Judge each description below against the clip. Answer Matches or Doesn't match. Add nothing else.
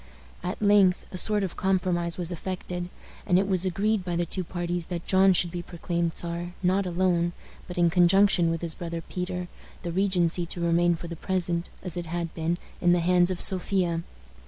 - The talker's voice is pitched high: Doesn't match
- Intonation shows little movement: Matches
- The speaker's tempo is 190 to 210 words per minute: Matches